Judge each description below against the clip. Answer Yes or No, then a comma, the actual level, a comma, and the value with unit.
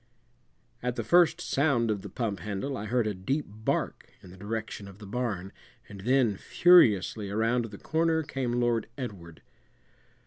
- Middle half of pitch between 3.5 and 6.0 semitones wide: Yes, average, 4.3 semitones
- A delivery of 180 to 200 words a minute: No, average, 165 wpm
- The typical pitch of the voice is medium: No, low, 115 Hz